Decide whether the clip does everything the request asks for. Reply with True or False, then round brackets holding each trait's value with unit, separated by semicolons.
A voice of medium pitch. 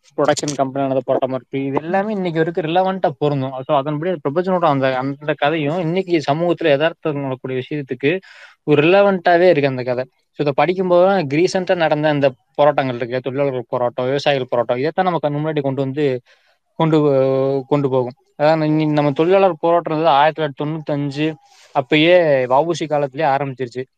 True (150 Hz)